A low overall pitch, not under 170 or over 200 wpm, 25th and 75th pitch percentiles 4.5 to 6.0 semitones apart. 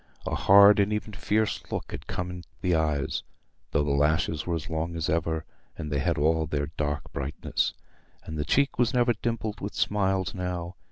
Yes: very low, 85 Hz; average, 190 wpm; average, 4.8 semitones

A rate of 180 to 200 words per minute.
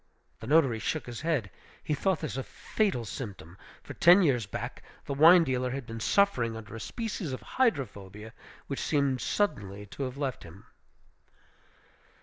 No: average, 160 wpm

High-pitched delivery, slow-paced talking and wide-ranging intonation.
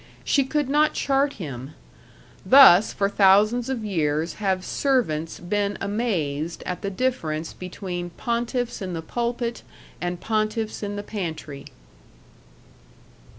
Yes: high, 200 Hz; slow, 120 wpm; wide, 5.7 semitones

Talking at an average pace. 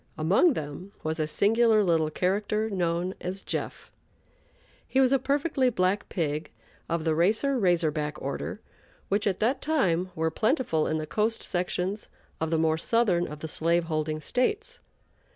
Yes: average, 160 wpm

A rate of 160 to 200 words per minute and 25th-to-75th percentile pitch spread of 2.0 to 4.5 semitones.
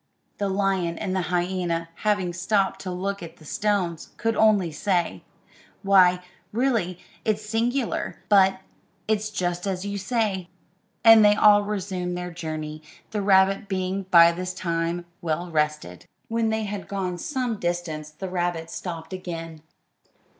No: average, 145 wpm; average, 3.0 semitones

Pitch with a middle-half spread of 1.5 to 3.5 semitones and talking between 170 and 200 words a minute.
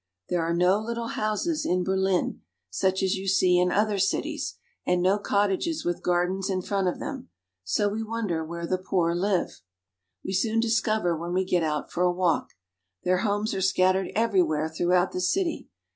Yes: average, 2.7 semitones; average, 180 wpm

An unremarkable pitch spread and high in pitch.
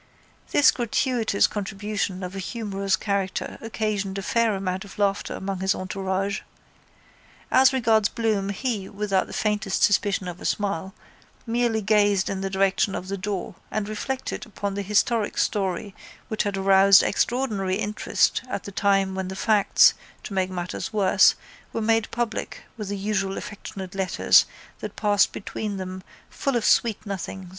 No: narrow, 2.0 semitones; high, 200 Hz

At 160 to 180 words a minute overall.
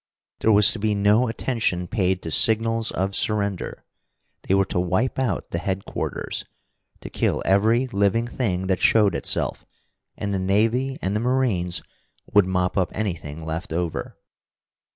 No: average, 150 wpm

